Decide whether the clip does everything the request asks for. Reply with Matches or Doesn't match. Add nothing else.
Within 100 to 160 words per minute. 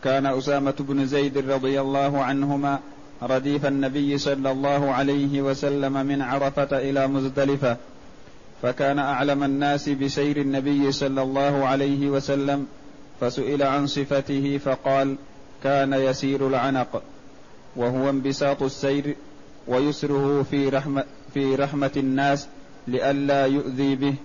Matches